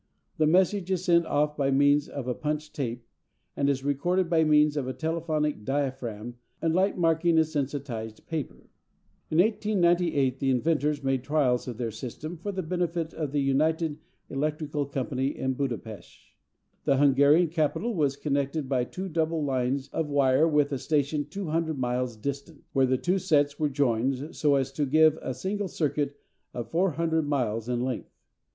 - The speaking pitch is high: No, medium, 145 Hz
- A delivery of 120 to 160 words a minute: No, average, 170 wpm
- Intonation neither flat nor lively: Yes, average, 3.3 semitones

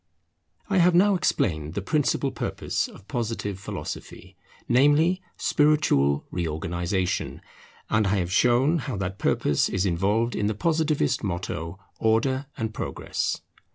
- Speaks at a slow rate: Yes, slow, 125 wpm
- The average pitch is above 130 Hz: No, low, 110 Hz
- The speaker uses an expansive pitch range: Yes, wide, 8.0 semitones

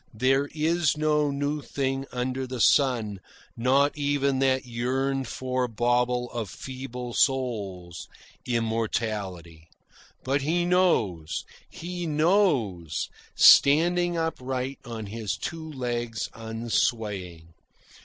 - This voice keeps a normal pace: No, slow, 100 wpm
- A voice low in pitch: Yes, low, 130 Hz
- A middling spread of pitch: Yes, average, 4.1 semitones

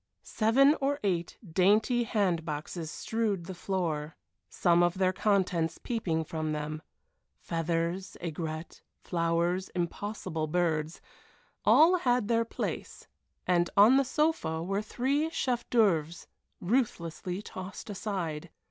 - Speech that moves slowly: Yes, slow, 110 wpm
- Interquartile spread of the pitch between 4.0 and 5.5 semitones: Yes, average, 4.9 semitones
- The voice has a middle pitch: Yes, medium, 180 Hz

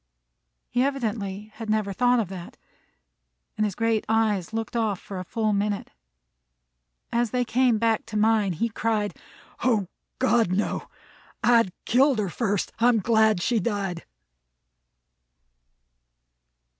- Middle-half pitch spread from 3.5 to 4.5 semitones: No, narrow, 2.4 semitones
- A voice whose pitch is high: Yes, high, 220 Hz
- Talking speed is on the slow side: Yes, slow, 130 wpm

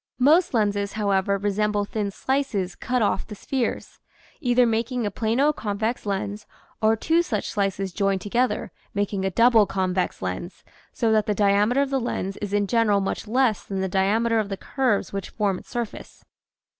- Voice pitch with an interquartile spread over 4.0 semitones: No, average, 3.0 semitones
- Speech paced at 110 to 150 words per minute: No, average, 175 wpm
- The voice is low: No, high, 210 Hz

